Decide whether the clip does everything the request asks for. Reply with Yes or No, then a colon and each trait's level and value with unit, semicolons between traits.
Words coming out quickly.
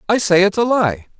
Yes: fast, 250 wpm